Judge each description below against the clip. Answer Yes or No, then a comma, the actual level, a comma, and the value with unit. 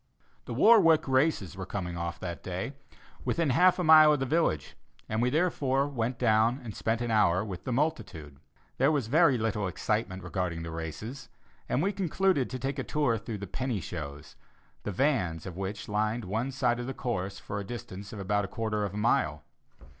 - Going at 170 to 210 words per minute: Yes, average, 195 wpm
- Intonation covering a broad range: Yes, wide, 6.1 semitones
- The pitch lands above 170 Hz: No, low, 115 Hz